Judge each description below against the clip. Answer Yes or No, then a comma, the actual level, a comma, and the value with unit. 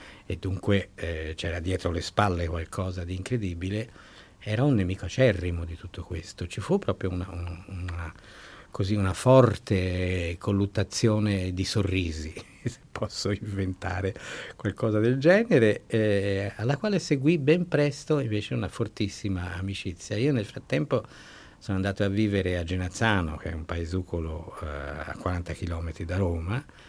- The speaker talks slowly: No, average, 145 wpm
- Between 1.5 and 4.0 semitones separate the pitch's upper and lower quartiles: Yes, average, 3.1 semitones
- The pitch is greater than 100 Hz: No, very low, 95 Hz